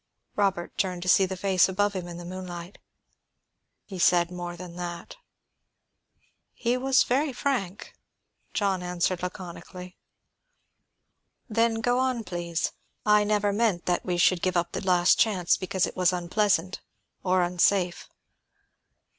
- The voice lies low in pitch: No, medium, 185 Hz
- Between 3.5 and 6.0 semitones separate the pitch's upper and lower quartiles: No, average, 2.8 semitones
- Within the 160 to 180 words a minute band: No, average, 140 wpm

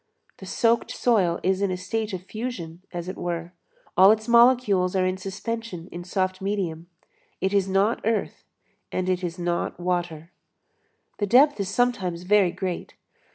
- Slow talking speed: No, average, 160 wpm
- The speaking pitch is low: No, high, 190 Hz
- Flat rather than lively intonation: No, average, 3.3 semitones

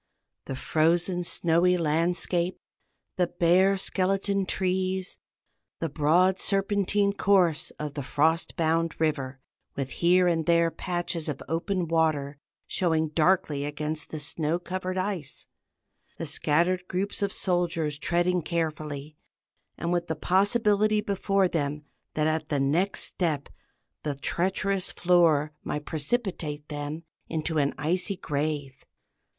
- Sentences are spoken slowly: Yes, slow, 125 wpm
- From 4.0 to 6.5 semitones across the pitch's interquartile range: No, average, 3.4 semitones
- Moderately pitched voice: Yes, medium, 170 Hz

